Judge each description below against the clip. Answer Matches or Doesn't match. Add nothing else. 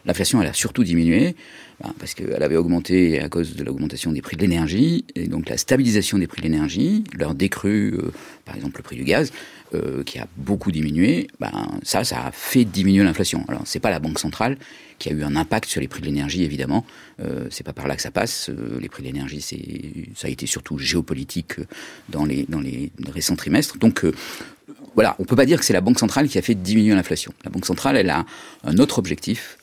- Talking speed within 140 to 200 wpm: Doesn't match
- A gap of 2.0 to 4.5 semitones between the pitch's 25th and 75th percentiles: Doesn't match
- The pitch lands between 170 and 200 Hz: Doesn't match